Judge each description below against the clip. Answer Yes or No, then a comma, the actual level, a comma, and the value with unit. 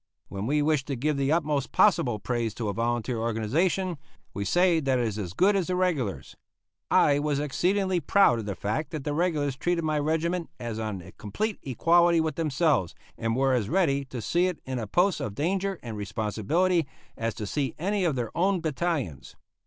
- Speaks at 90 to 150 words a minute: No, average, 200 wpm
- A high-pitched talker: No, medium, 145 Hz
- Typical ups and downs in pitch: No, wide, 7.0 semitones